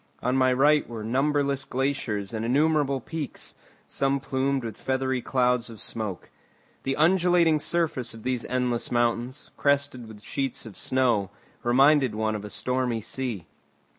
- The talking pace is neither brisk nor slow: Yes, average, 145 wpm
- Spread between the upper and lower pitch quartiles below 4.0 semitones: Yes, average, 3.1 semitones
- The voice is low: Yes, low, 130 Hz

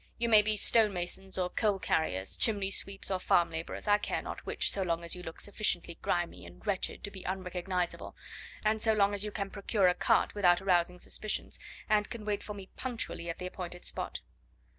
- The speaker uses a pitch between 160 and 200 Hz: Yes, high, 190 Hz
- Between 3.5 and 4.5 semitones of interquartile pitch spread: No, average, 2.8 semitones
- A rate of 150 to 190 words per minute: No, fast, 205 wpm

